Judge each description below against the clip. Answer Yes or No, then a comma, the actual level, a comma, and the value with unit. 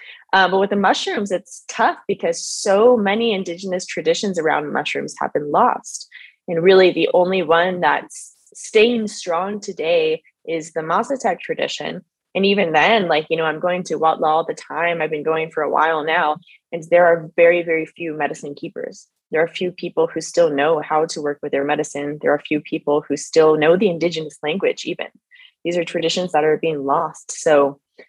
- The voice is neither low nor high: Yes, medium, 170 Hz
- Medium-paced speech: Yes, average, 190 wpm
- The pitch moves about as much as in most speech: Yes, average, 4.4 semitones